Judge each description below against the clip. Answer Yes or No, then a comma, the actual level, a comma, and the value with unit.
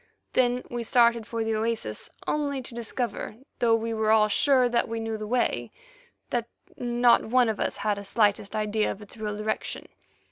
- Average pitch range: No, narrow, 2.0 semitones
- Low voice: No, high, 225 Hz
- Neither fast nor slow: Yes, average, 185 wpm